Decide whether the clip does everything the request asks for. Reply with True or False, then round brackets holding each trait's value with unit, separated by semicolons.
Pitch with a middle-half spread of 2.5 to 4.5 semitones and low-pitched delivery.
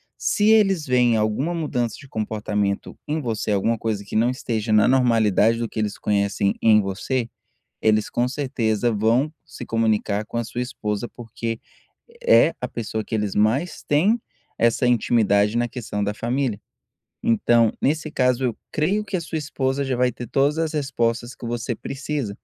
True (3.9 semitones; 120 Hz)